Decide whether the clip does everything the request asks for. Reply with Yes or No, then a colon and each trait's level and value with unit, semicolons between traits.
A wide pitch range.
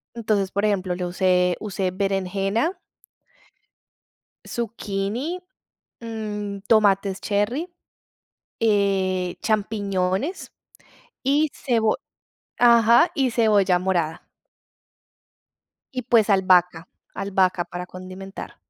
No: average, 3.3 semitones